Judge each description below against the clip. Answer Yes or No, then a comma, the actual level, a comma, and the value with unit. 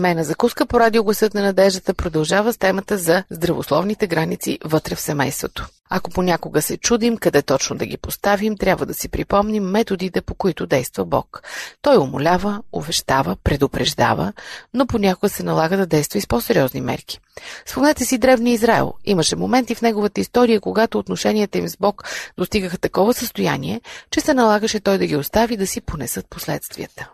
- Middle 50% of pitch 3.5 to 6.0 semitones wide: Yes, average, 4.9 semitones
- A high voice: Yes, high, 200 Hz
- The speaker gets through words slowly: No, fast, 165 wpm